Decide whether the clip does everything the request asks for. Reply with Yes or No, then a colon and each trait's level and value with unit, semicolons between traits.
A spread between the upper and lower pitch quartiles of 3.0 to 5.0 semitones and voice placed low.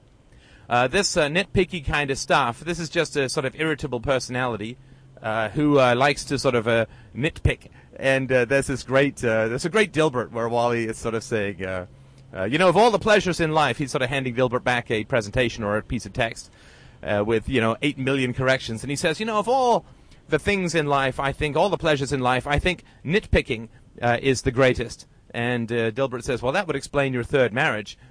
Yes: average, 4.0 semitones; low, 130 Hz